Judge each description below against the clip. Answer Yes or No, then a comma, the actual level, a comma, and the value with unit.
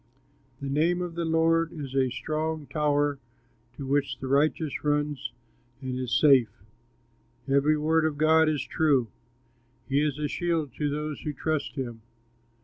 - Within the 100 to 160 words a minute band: Yes, average, 150 wpm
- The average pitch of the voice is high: No, medium, 150 Hz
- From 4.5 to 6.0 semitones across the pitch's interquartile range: No, narrow, 2.4 semitones